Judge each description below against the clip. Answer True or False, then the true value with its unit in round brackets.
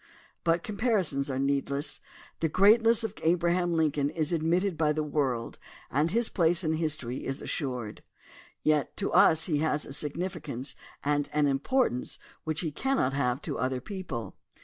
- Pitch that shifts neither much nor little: True (4.0 semitones)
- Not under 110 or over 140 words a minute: False (160 wpm)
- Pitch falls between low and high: True (155 Hz)